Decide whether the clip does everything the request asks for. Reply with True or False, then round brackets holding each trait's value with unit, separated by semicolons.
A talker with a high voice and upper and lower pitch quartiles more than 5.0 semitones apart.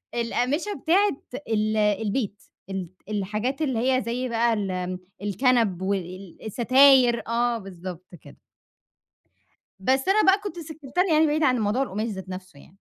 True (230 Hz; 5.4 semitones)